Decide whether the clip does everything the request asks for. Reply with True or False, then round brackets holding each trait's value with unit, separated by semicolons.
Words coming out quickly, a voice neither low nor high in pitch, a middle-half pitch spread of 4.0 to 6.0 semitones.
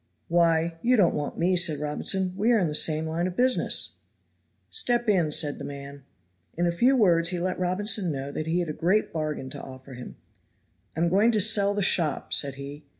True (210 wpm; 170 Hz; 4.3 semitones)